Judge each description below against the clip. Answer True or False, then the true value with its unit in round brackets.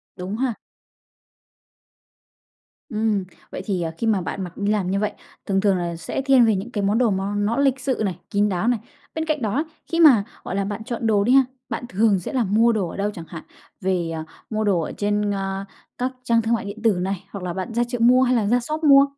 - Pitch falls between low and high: False (210 Hz)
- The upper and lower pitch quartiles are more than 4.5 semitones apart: False (3.7 semitones)